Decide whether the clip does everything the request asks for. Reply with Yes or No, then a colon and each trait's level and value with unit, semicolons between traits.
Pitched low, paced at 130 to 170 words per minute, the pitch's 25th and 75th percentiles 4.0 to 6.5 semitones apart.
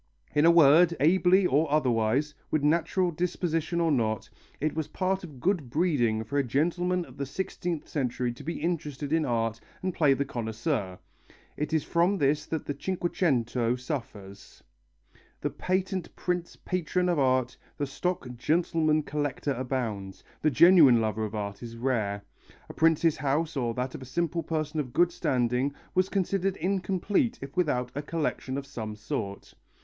No: medium, 150 Hz; average, 165 wpm; wide, 5.5 semitones